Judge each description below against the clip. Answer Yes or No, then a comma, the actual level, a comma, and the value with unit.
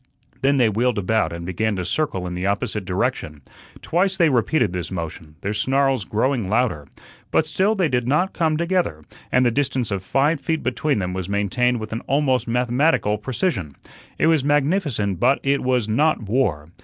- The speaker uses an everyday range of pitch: No, wide, 6.4 semitones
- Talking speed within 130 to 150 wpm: No, average, 180 wpm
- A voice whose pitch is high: No, low, 125 Hz